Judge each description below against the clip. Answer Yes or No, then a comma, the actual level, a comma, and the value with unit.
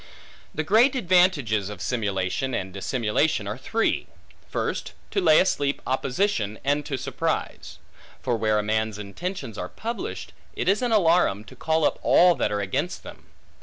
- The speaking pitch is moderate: No, low, 130 Hz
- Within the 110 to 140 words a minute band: No, average, 160 wpm